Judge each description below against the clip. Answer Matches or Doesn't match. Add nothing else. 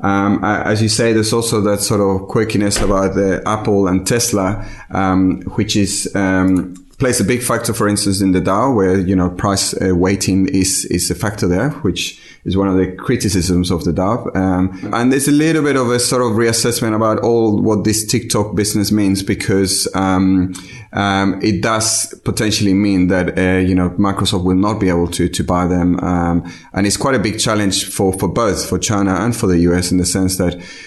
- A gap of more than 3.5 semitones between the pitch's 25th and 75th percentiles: Doesn't match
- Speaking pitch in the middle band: Doesn't match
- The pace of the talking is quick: Matches